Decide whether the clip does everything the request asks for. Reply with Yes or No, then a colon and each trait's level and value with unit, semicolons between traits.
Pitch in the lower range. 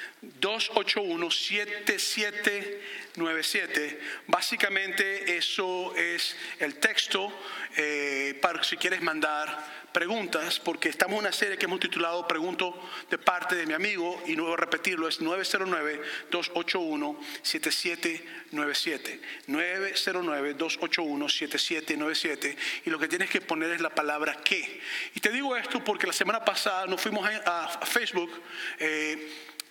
No: medium, 180 Hz